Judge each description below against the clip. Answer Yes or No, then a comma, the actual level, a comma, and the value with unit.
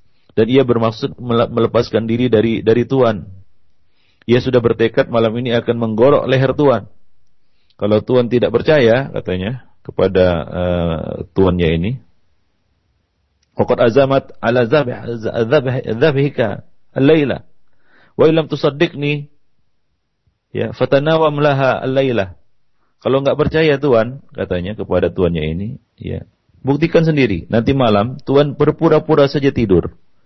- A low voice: Yes, low, 120 Hz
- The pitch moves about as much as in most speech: No, wide, 5.8 semitones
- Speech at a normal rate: Yes, average, 100 wpm